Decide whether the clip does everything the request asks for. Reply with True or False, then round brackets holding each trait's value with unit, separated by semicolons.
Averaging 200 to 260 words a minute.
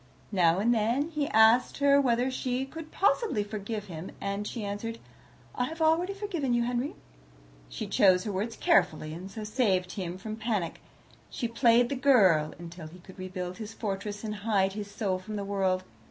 False (185 wpm)